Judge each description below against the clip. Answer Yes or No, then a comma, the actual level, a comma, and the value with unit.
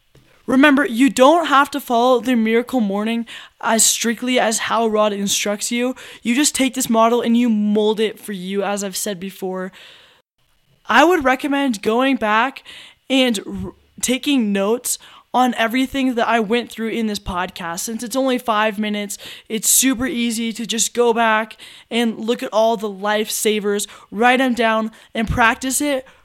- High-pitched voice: Yes, high, 230 Hz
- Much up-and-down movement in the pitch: No, average, 3.3 semitones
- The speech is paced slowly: No, average, 165 wpm